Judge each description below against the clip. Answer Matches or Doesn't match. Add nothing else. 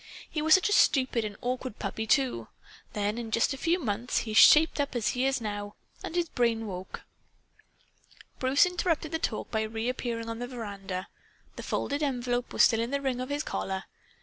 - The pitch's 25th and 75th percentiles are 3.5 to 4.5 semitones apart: Matches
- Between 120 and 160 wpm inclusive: Doesn't match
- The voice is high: Matches